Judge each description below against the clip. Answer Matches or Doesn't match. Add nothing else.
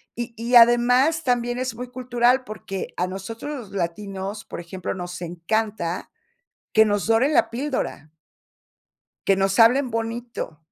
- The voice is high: Matches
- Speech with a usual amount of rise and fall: Matches